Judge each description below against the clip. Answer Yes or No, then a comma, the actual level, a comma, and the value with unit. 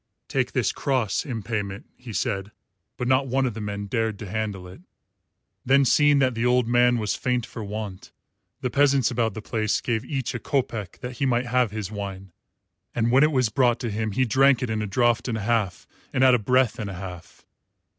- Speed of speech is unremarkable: No, fast, 215 wpm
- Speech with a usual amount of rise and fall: Yes, average, 3.4 semitones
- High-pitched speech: No, low, 115 Hz